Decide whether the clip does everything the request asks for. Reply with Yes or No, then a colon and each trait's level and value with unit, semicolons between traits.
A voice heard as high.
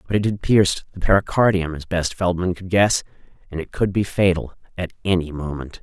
No: very low, 90 Hz